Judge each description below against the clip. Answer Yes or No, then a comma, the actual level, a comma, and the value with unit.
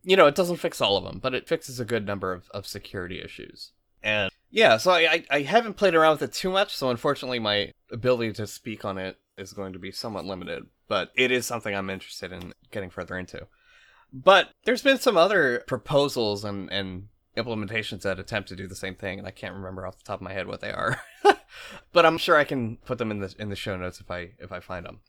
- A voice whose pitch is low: Yes, low, 110 Hz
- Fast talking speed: Yes, fast, 245 wpm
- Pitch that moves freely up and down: Yes, wide, 6.4 semitones